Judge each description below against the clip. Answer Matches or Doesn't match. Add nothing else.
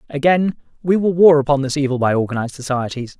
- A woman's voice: Doesn't match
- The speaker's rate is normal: Matches